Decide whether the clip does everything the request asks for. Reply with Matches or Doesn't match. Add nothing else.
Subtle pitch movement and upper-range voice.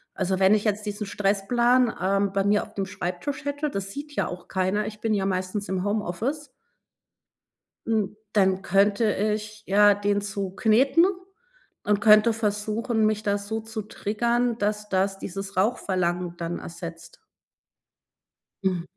Matches